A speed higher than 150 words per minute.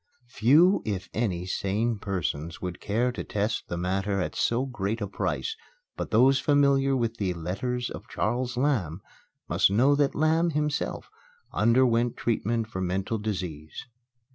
No: average, 145 wpm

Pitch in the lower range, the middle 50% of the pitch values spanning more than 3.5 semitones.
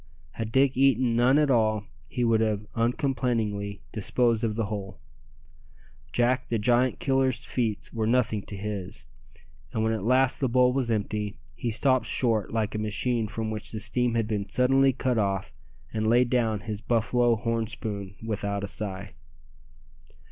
No: low, 115 Hz; average, 2.8 semitones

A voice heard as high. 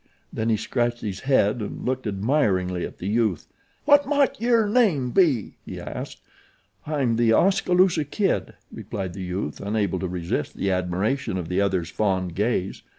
No: low, 110 Hz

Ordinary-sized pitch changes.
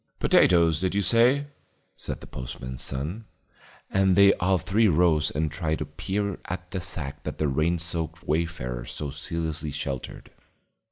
Yes: average, 4.0 semitones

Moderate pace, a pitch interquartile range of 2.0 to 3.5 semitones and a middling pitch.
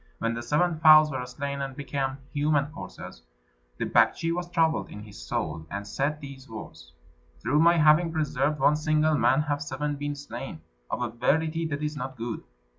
Yes: average, 185 wpm; average, 2.8 semitones; medium, 145 Hz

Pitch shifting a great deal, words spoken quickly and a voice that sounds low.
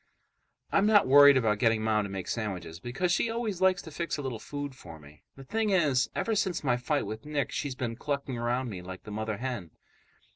Yes: wide, 5.8 semitones; fast, 220 wpm; low, 130 Hz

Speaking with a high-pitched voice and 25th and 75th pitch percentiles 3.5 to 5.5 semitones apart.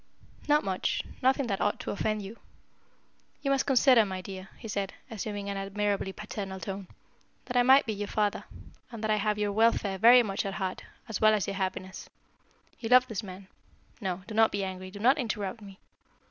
No: high, 205 Hz; average, 2.7 semitones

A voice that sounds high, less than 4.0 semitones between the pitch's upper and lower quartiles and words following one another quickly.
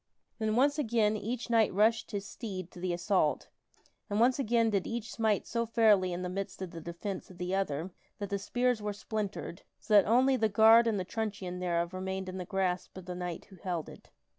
Yes: high, 200 Hz; average, 3.5 semitones; fast, 215 wpm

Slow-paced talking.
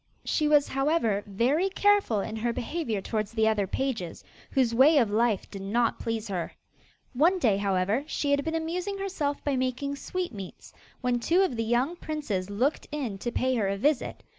No: average, 185 wpm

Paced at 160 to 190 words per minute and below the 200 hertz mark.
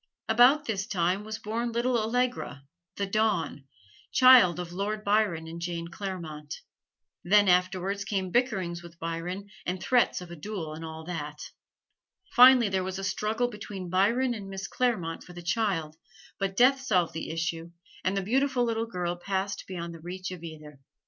Yes: average, 170 wpm; high, 190 Hz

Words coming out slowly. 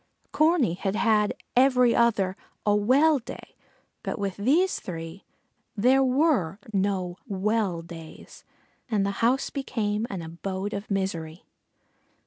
Yes: slow, 120 wpm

